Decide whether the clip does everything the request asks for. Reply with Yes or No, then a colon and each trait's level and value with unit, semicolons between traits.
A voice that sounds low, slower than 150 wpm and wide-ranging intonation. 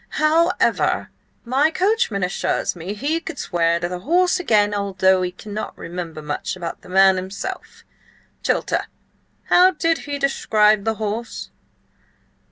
No: high, 210 Hz; slow, 135 wpm; wide, 8.8 semitones